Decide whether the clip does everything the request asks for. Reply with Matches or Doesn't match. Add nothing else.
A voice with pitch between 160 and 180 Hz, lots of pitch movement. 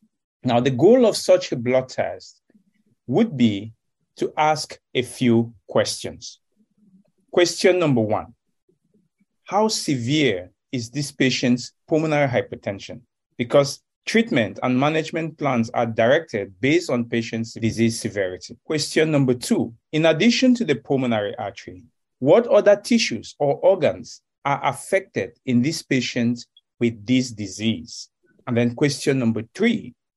Doesn't match